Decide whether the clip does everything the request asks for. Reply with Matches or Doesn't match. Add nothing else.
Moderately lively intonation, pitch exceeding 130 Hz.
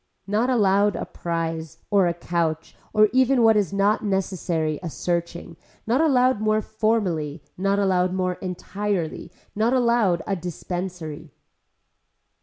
Matches